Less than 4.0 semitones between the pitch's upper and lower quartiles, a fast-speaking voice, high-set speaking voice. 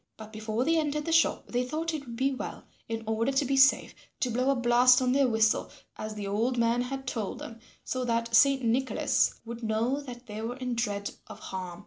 Yes: average, 3.1 semitones; fast, 225 wpm; high, 245 Hz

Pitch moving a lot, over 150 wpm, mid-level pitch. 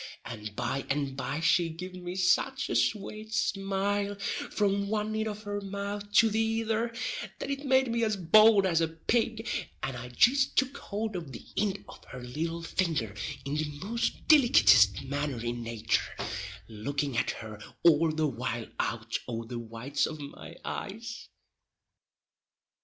Yes: wide, 8.3 semitones; average, 160 wpm; medium, 175 Hz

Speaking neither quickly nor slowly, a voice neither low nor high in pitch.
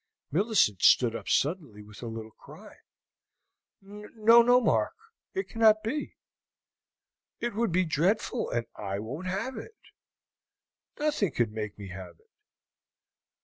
No: slow, 130 wpm; medium, 180 Hz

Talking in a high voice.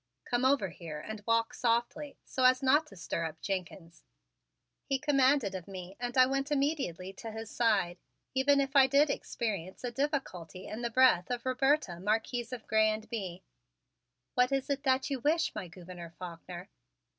Yes: high, 235 Hz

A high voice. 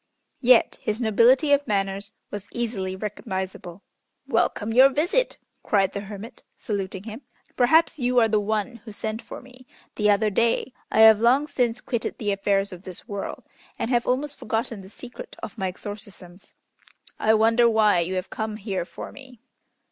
Yes: high, 220 Hz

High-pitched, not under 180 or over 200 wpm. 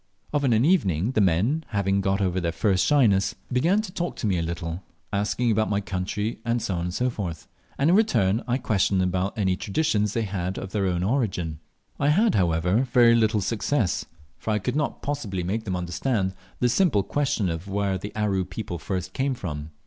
No: low, 100 Hz; average, 190 wpm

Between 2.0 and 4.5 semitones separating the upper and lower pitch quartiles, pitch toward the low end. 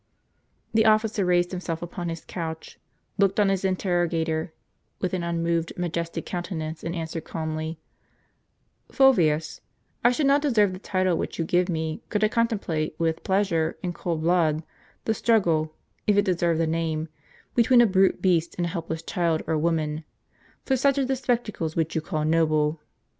No: average, 3.5 semitones; medium, 170 Hz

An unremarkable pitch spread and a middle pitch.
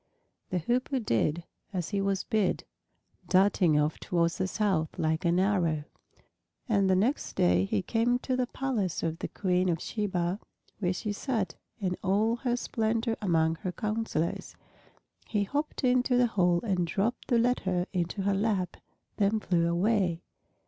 No: average, 4.5 semitones; high, 195 Hz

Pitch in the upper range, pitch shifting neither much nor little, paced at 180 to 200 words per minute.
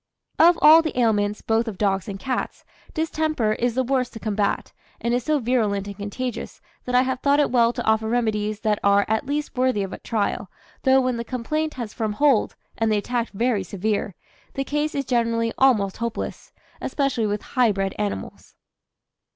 Yes: high, 230 Hz; average, 3.7 semitones; average, 190 wpm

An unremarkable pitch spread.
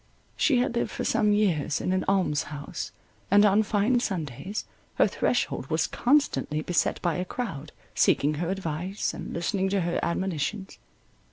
Yes: average, 4.1 semitones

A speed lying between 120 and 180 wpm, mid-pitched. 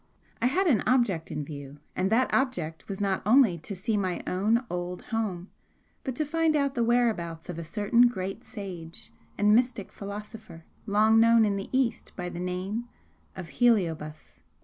No: average, 170 wpm; high, 205 Hz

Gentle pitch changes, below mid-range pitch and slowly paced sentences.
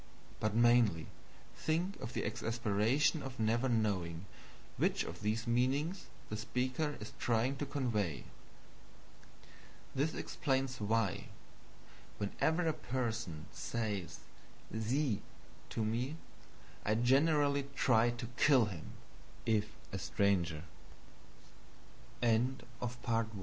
No: average, 3.9 semitones; low, 115 Hz; slow, 105 wpm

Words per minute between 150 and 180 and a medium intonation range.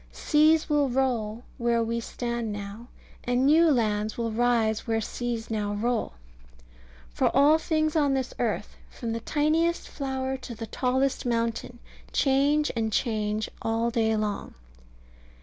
No: average, 140 wpm; average, 3.5 semitones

